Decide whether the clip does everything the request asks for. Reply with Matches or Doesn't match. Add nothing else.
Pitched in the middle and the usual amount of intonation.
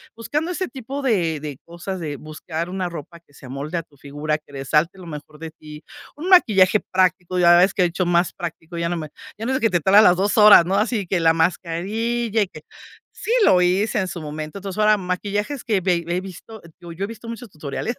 Matches